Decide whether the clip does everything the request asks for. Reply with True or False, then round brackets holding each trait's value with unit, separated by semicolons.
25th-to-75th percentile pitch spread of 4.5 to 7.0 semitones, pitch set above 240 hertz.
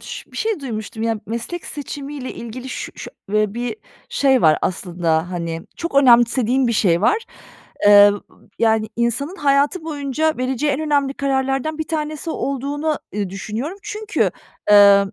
True (5.4 semitones; 260 Hz)